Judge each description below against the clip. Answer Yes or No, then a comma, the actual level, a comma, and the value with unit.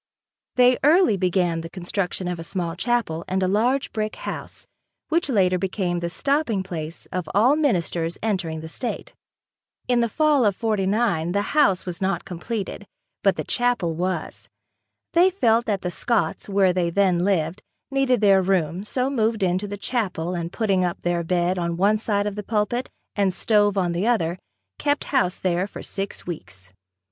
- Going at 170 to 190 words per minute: Yes, average, 175 wpm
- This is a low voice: No, high, 195 Hz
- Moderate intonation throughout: Yes, average, 4.5 semitones